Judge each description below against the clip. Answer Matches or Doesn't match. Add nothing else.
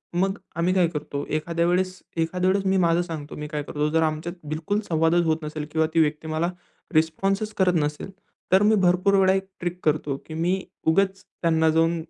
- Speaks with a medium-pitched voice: Matches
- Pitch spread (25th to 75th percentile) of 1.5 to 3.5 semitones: Matches